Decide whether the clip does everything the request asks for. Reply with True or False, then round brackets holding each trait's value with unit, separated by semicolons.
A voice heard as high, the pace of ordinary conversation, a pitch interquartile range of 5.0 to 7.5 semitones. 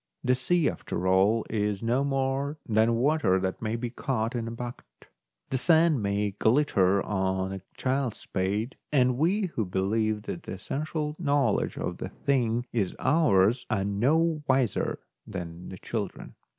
False (115 Hz; 155 wpm; 5.4 semitones)